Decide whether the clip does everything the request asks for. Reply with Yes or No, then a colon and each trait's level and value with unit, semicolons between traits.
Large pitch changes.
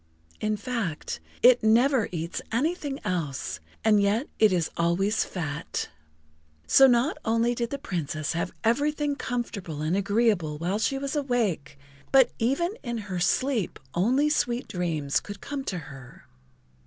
Yes: wide, 6.6 semitones